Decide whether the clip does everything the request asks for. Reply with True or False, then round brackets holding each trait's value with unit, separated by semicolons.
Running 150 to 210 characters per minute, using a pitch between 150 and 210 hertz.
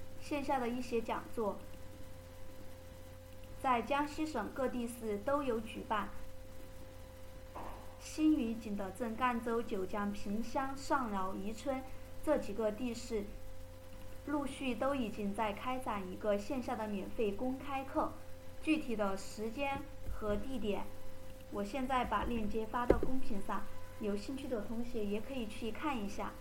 False (200 characters per minute; 220 Hz)